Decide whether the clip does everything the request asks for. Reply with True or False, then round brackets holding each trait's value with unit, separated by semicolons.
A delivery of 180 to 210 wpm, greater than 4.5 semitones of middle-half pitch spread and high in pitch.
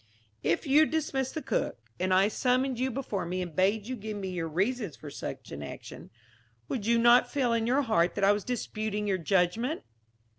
True (200 wpm; 5.3 semitones; 215 Hz)